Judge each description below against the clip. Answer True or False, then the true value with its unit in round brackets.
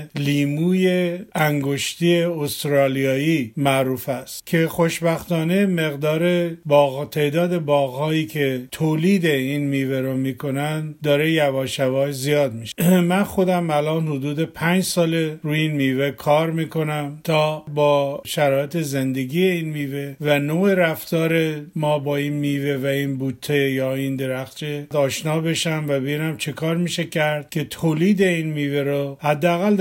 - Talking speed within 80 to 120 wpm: False (130 wpm)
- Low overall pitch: False (150 Hz)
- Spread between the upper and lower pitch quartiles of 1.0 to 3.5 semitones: True (2.6 semitones)